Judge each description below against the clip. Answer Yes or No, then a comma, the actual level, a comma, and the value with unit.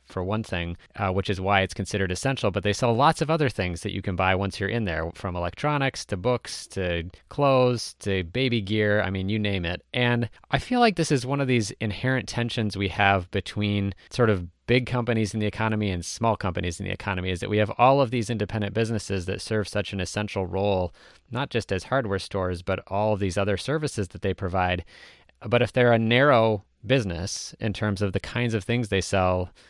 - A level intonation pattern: No, average, 3.9 semitones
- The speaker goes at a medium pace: No, fast, 220 wpm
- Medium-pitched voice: No, low, 105 Hz